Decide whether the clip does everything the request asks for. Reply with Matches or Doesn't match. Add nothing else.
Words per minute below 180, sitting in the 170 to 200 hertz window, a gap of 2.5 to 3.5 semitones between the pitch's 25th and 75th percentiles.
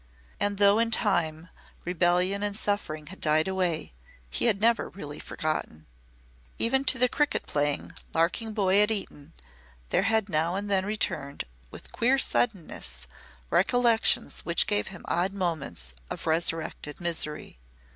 Doesn't match